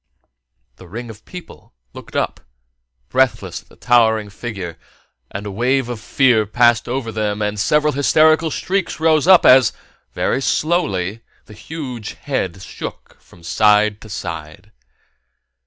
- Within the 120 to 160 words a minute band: Yes, average, 140 wpm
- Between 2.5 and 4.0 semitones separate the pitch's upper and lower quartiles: No, average, 4.6 semitones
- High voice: No, low, 115 Hz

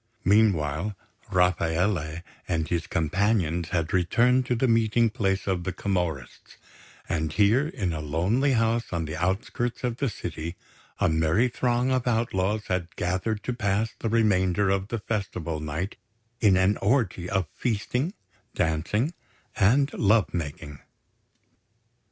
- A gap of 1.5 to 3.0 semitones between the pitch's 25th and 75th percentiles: No, average, 5.2 semitones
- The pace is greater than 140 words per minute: No, slow, 135 wpm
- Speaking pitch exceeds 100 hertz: No, very low, 95 Hz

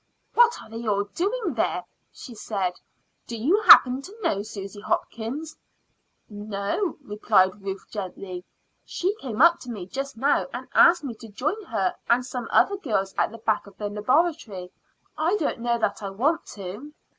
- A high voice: Yes, high, 230 Hz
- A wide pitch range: Yes, wide, 6.9 semitones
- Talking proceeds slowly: No, average, 170 wpm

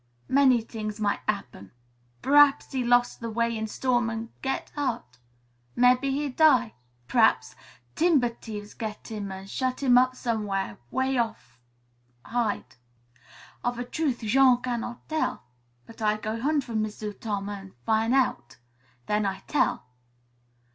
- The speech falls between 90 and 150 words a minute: Yes, average, 140 wpm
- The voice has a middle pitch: No, high, 235 Hz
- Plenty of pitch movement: No, average, 3.2 semitones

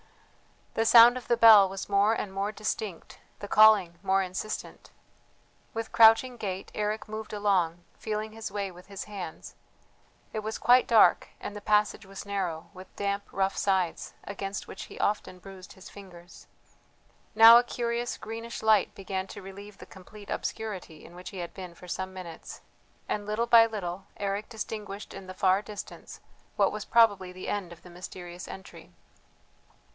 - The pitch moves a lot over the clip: No, narrow, 2.5 semitones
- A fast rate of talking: No, average, 170 wpm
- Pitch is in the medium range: No, high, 200 Hz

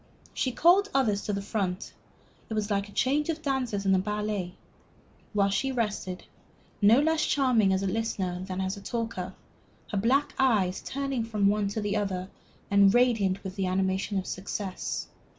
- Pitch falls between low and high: No, high, 205 Hz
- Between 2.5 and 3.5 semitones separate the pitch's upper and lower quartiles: No, average, 3.9 semitones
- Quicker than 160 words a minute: Yes, average, 170 wpm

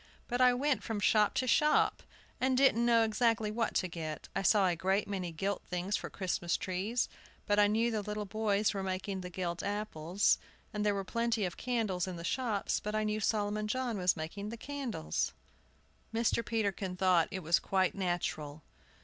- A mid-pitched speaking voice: No, high, 205 Hz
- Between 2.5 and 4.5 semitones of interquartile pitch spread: Yes, average, 3.5 semitones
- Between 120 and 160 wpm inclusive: No, average, 185 wpm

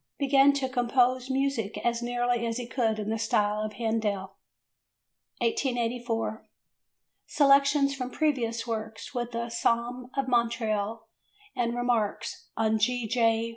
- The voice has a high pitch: Yes, high, 235 Hz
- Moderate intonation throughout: No, narrow, 2.1 semitones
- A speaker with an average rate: No, slow, 130 wpm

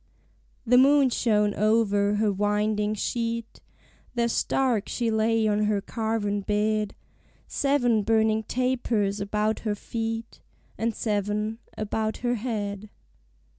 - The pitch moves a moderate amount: No, narrow, 1.8 semitones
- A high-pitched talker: Yes, high, 220 Hz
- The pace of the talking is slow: Yes, slow, 115 wpm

